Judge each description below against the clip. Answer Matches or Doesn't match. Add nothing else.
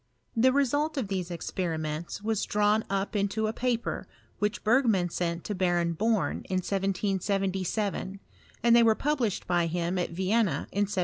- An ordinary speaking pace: Matches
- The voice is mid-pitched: Doesn't match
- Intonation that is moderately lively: Matches